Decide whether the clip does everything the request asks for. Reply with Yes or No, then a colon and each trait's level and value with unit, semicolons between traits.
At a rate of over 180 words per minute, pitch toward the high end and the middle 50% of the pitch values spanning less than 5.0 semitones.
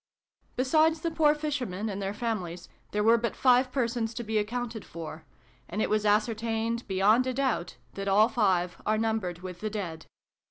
No: average, 175 wpm; high, 220 Hz; average, 3.8 semitones